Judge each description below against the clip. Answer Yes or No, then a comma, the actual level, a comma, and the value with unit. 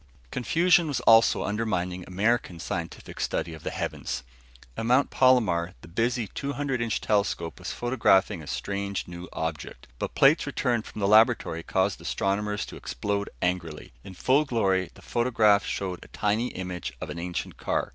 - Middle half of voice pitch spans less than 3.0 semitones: No, average, 5.0 semitones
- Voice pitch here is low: Yes, low, 100 Hz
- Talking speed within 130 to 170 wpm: Yes, average, 160 wpm